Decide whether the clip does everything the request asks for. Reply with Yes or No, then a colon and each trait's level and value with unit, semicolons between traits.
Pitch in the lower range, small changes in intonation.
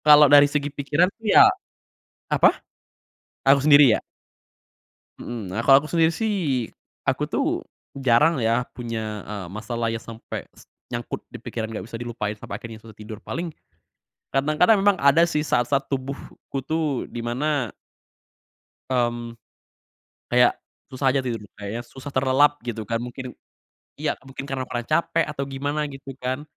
No: low, 130 Hz; average, 3.7 semitones